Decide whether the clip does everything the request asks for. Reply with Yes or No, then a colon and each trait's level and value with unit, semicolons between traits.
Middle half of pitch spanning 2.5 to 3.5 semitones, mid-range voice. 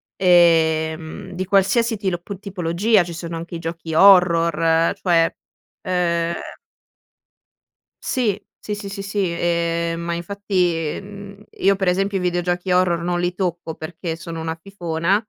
Yes: average, 2.8 semitones; medium, 175 Hz